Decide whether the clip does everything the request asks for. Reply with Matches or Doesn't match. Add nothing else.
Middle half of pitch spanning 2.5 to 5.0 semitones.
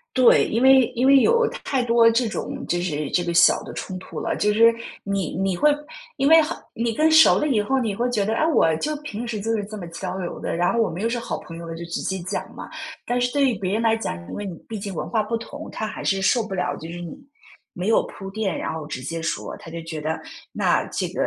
Doesn't match